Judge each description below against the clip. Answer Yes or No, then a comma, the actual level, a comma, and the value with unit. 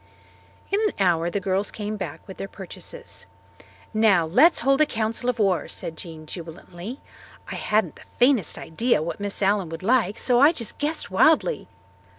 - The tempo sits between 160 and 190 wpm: Yes, average, 170 wpm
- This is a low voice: No, high, 210 Hz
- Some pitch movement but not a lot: No, wide, 5.7 semitones